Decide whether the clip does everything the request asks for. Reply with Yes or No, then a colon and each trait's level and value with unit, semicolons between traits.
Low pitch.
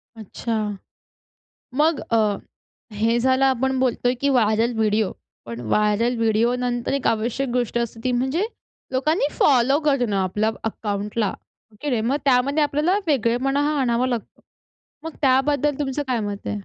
No: high, 245 Hz